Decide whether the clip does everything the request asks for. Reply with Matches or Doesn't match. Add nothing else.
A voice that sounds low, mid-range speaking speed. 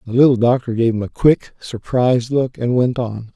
Doesn't match